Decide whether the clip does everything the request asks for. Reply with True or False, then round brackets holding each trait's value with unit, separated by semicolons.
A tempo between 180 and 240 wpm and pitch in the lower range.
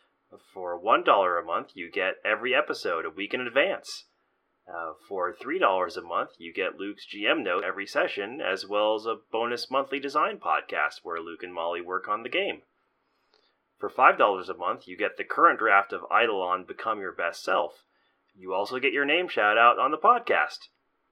True (185 wpm; 100 Hz)